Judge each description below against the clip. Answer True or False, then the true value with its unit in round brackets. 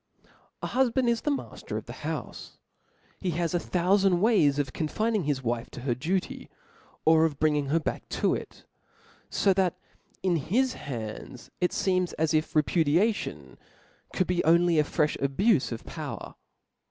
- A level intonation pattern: False (4.7 semitones)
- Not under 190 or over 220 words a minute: False (165 wpm)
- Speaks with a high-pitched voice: False (170 Hz)